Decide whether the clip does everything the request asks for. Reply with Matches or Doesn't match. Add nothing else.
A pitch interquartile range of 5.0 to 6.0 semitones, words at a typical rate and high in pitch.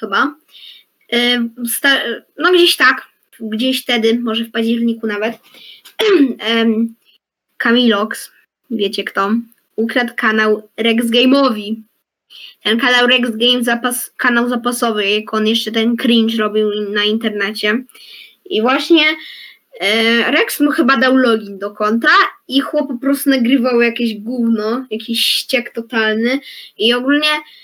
Doesn't match